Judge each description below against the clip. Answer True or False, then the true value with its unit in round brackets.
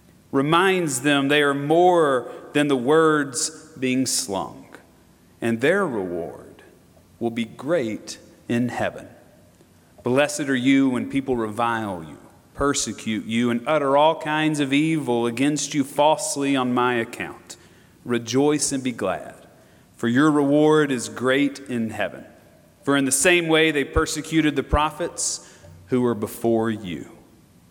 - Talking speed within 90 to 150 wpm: True (135 wpm)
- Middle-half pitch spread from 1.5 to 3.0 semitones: False (4.2 semitones)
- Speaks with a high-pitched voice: False (135 Hz)